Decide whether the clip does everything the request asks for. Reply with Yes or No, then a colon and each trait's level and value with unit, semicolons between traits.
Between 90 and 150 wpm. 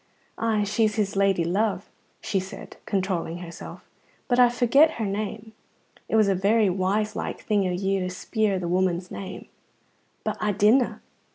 No: average, 165 wpm